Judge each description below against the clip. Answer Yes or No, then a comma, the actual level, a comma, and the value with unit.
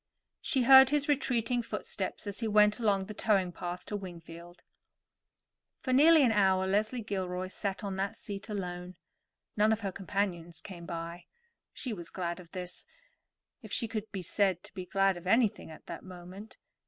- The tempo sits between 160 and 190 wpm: Yes, average, 175 wpm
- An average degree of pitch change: Yes, average, 3.5 semitones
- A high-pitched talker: Yes, high, 195 Hz